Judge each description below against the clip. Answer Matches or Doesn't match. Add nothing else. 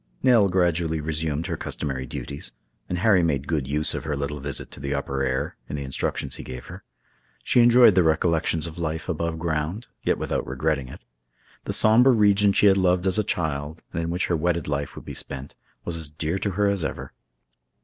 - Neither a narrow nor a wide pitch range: Matches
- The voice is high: Doesn't match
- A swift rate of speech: Matches